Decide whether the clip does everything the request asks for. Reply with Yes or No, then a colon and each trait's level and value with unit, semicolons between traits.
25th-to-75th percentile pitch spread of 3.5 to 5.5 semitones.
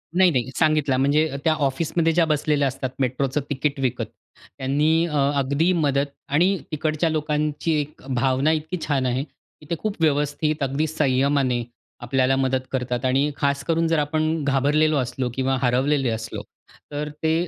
No: average, 2.7 semitones